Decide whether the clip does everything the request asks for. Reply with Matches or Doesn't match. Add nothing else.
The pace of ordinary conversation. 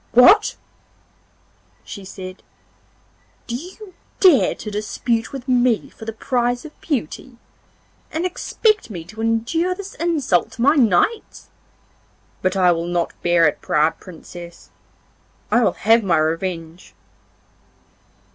Doesn't match